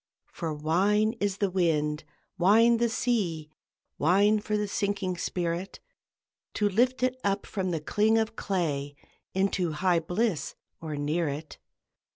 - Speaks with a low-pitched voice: No, high, 190 Hz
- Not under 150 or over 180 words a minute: No, average, 140 wpm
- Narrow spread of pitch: No, average, 4.4 semitones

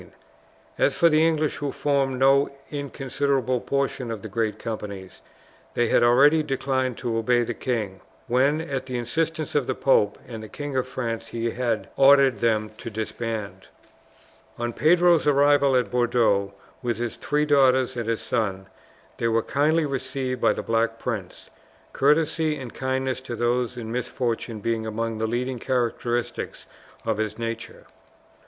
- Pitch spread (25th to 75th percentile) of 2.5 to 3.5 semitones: Yes, average, 3.2 semitones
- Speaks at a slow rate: No, average, 155 wpm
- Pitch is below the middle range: Yes, low, 125 Hz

